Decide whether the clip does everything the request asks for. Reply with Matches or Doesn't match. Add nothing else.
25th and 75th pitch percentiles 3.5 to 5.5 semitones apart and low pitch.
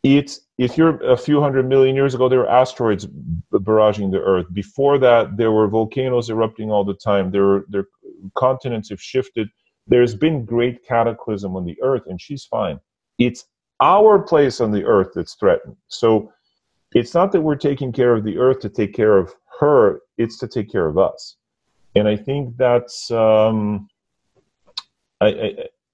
Matches